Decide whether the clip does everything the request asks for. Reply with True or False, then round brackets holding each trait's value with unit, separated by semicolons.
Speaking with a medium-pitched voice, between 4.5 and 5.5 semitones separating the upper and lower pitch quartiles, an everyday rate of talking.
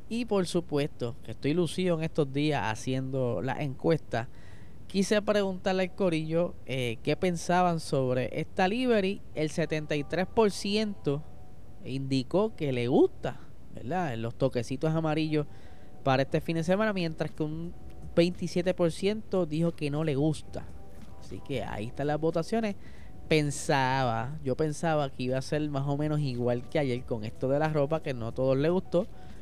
True (155 Hz; 4.9 semitones; 155 wpm)